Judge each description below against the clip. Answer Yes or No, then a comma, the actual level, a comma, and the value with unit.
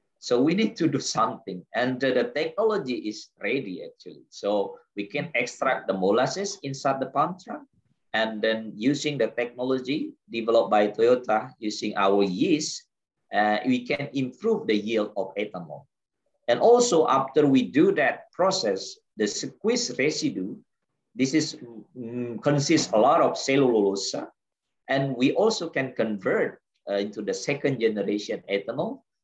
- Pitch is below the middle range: Yes, low, 130 Hz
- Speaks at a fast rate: Yes, fast, 145 wpm